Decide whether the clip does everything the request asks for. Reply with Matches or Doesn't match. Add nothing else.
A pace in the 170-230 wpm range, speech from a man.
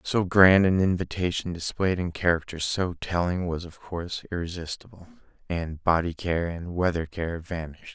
Doesn't match